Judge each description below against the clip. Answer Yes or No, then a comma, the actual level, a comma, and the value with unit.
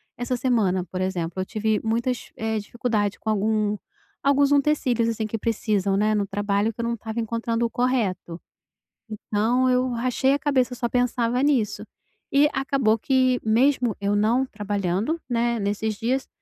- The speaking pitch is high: Yes, high, 230 Hz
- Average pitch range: Yes, average, 3.3 semitones